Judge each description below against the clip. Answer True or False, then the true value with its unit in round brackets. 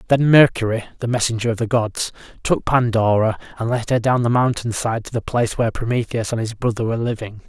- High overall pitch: False (115 Hz)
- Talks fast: True (210 wpm)